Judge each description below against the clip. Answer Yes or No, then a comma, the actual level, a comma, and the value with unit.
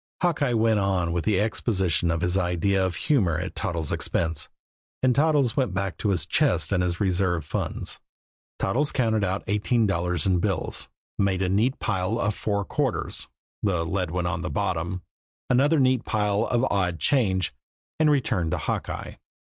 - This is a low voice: Yes, very low, 95 Hz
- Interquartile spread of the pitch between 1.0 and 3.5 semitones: No, average, 4.3 semitones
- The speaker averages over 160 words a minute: Yes, average, 170 wpm